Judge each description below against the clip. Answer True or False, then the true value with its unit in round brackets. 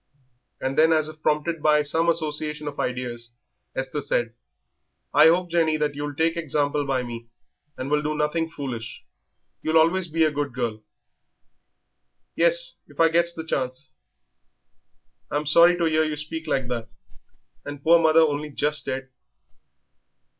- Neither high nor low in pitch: True (150 Hz)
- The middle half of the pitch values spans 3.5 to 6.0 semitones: False (2.8 semitones)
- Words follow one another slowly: False (155 wpm)